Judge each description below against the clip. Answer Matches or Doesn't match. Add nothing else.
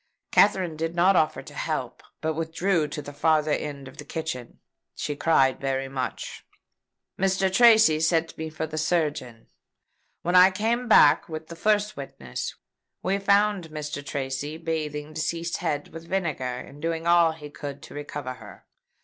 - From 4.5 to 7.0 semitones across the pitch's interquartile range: Doesn't match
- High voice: Doesn't match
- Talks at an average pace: Matches